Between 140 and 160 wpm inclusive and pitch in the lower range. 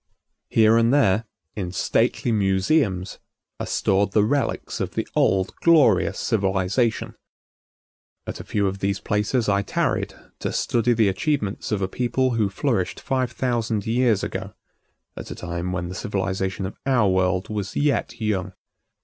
Yes: average, 150 wpm; low, 105 Hz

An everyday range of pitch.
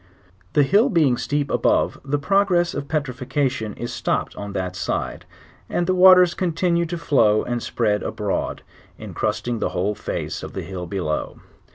No: wide, 8.4 semitones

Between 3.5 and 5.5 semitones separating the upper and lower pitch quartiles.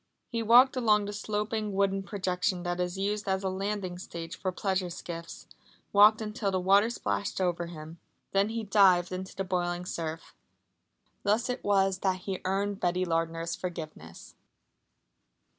No: narrow, 2.5 semitones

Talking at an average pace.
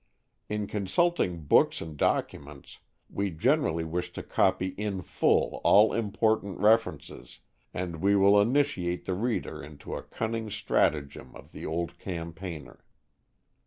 No: slow, 125 wpm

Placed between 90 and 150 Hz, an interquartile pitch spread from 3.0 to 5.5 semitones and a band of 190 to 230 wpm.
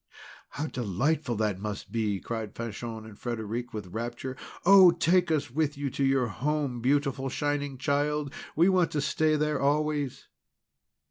No: low, 135 Hz; average, 4.4 semitones; average, 150 wpm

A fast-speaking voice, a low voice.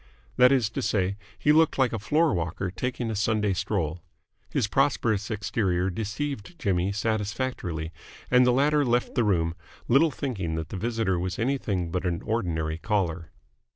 No: average, 155 wpm; low, 105 Hz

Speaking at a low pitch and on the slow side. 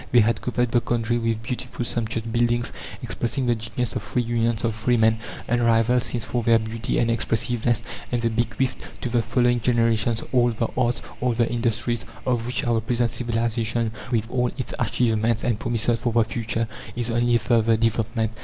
No: low, 115 Hz; average, 185 wpm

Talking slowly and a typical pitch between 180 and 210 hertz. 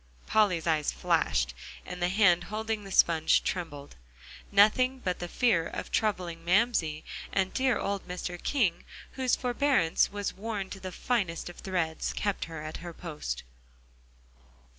No: average, 145 wpm; medium, 185 Hz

